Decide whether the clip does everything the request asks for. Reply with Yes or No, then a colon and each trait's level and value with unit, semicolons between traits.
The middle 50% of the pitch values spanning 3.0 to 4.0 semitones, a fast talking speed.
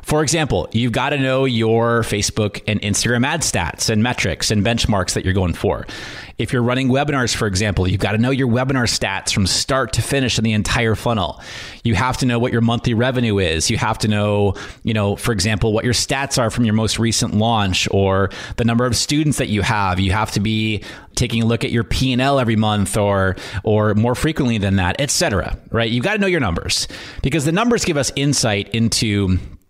Yes: average, 3.6 semitones; fast, 230 wpm